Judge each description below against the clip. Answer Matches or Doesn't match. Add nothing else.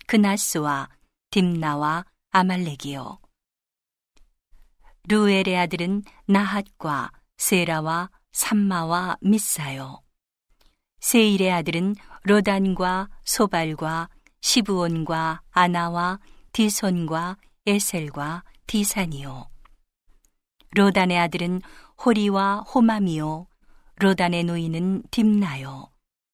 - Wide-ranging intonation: Doesn't match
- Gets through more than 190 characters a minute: Doesn't match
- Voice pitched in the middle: Matches